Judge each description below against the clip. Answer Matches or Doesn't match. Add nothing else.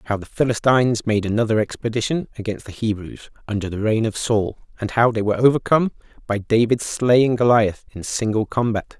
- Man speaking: Matches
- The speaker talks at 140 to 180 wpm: Matches